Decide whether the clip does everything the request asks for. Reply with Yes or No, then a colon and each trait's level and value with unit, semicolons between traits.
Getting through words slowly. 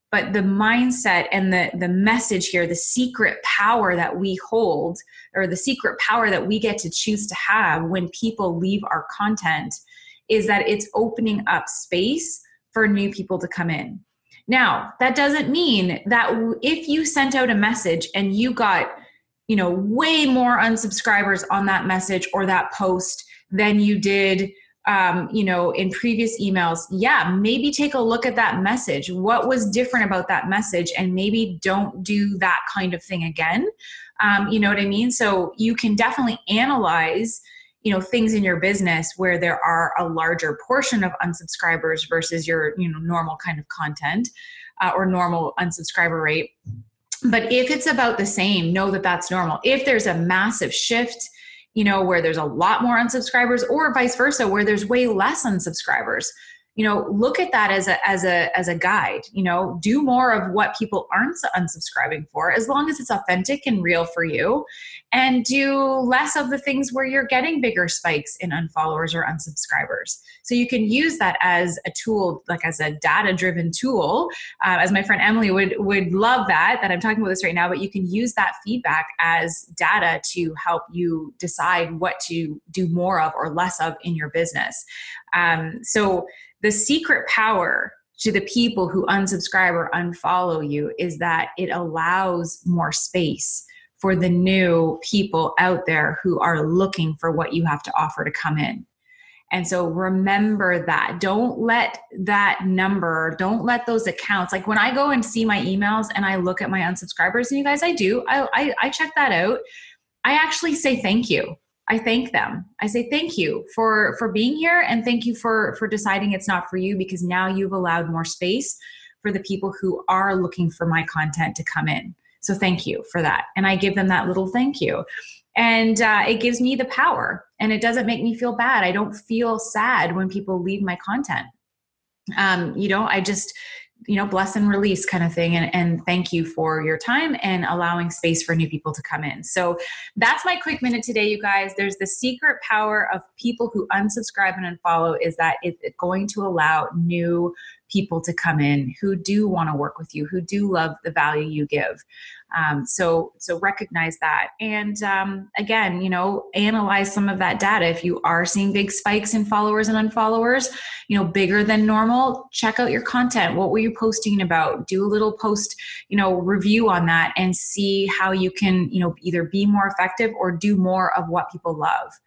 No: average, 195 wpm